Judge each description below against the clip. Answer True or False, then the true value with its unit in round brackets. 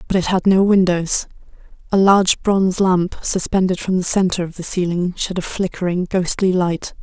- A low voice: False (185 Hz)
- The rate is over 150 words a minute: True (170 wpm)